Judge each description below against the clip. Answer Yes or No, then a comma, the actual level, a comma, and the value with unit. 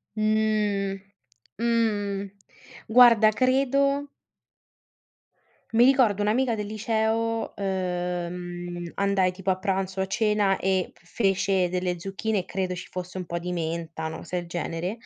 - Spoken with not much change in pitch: No, average, 3.4 semitones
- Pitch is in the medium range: No, high, 195 Hz